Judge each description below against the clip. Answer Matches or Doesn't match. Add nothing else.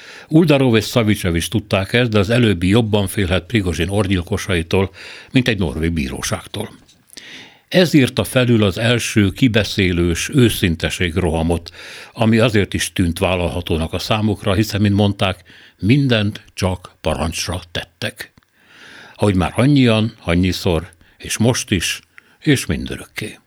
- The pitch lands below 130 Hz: Matches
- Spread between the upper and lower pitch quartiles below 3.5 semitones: Doesn't match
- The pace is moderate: Matches